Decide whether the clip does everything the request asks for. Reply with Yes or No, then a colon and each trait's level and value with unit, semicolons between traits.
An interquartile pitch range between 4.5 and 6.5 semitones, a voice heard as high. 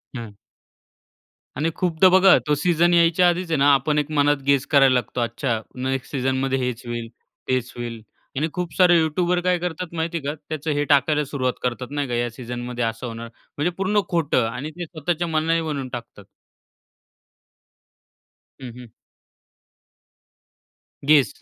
No: average, 4.8 semitones; medium, 145 Hz